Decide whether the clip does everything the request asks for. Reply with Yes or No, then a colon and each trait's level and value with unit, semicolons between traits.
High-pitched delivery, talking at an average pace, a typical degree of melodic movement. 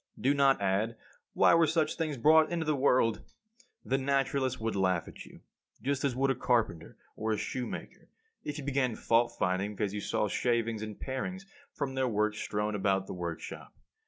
No: low, 120 Hz; average, 185 wpm; average, 4.8 semitones